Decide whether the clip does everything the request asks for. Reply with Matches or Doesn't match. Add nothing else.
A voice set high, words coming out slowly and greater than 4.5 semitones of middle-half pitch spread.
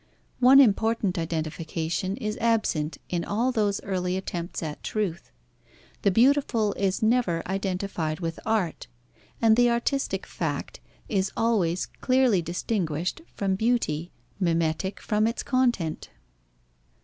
Matches